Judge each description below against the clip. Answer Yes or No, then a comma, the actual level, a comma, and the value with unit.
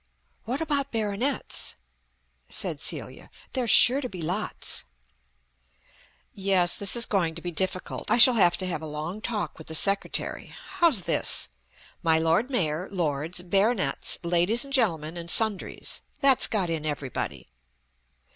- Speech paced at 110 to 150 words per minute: Yes, average, 145 wpm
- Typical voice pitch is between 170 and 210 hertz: Yes, high, 190 Hz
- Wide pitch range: Yes, wide, 5.7 semitones